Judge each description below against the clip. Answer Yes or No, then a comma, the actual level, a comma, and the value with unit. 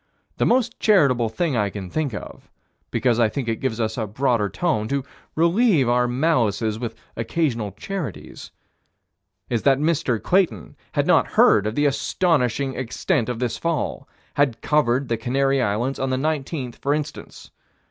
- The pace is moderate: Yes, average, 160 wpm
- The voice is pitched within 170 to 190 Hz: No, low, 130 Hz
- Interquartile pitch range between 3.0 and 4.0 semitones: No, average, 4.8 semitones